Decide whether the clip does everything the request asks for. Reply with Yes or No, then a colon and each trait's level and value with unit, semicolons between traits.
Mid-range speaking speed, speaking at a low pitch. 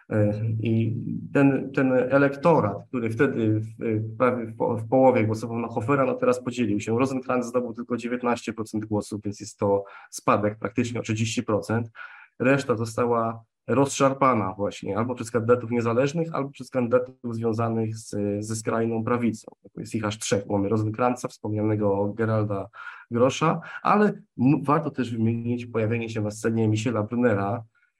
Yes: average, 140 wpm; low, 115 Hz